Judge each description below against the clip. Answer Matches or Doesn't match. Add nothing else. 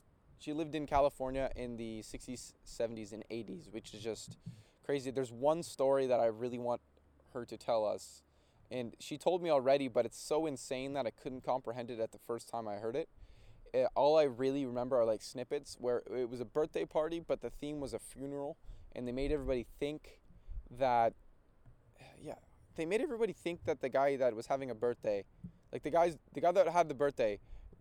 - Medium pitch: Doesn't match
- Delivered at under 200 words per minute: Doesn't match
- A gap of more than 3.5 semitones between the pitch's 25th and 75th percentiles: Matches